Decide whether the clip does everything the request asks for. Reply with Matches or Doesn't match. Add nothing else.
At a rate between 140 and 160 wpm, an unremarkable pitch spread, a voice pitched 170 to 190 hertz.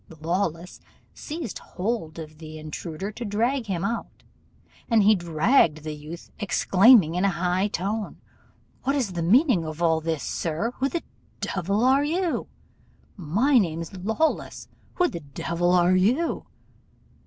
Doesn't match